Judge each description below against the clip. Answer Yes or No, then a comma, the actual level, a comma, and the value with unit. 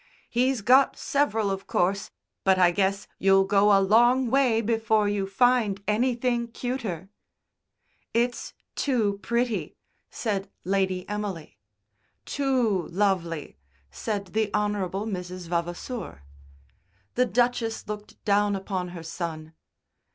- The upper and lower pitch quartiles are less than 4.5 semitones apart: Yes, average, 3.7 semitones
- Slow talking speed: Yes, slow, 115 wpm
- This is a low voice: No, high, 205 Hz